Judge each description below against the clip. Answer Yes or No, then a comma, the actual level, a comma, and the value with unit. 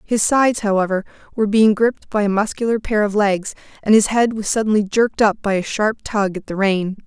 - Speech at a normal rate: No, fast, 220 wpm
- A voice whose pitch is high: Yes, high, 210 Hz